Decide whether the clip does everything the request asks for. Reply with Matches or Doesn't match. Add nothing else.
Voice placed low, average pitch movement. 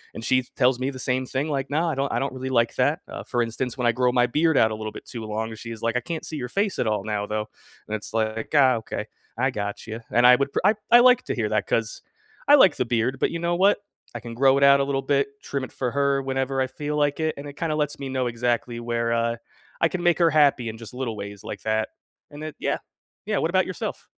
Matches